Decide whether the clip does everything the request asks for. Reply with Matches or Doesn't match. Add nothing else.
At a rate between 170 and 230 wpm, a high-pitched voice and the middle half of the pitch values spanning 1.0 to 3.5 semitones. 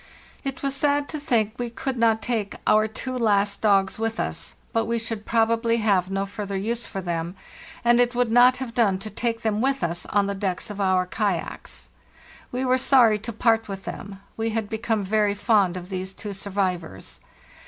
Matches